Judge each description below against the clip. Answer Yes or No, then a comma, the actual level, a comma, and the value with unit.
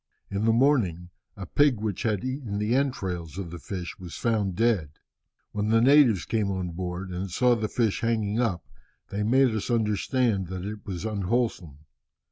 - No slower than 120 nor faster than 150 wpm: No, average, 175 wpm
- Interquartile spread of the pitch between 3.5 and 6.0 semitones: Yes, average, 4.2 semitones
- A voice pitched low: Yes, low, 105 Hz